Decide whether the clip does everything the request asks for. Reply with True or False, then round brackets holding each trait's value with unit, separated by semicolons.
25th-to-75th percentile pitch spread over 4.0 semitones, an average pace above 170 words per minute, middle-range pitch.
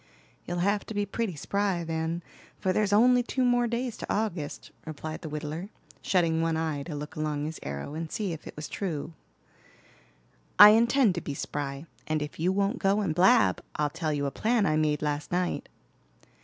True (5.1 semitones; 195 wpm; 165 Hz)